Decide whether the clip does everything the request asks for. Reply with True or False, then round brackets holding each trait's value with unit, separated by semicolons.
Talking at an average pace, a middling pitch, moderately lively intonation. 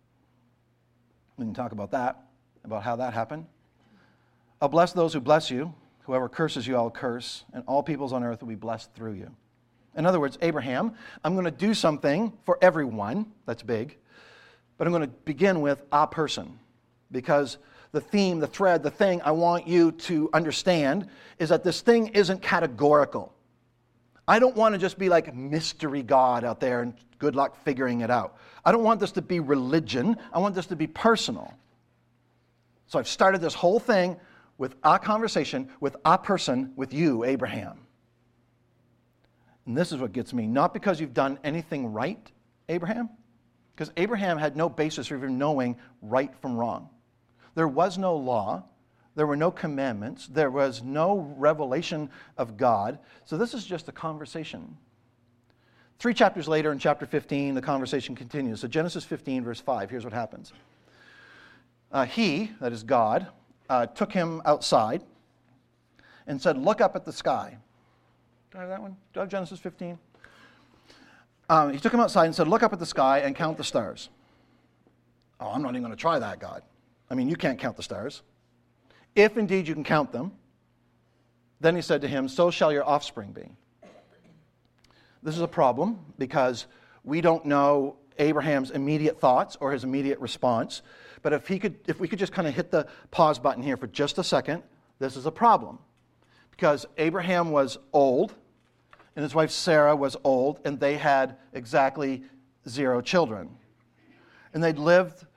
True (175 wpm; 150 Hz; 5.0 semitones)